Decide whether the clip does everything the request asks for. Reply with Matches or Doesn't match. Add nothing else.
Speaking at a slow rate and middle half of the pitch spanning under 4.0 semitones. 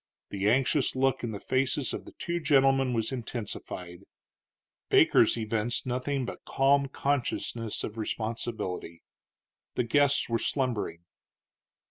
Matches